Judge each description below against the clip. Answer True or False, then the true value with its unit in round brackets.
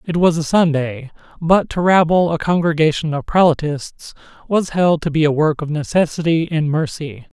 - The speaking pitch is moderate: True (160 Hz)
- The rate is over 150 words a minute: True (170 wpm)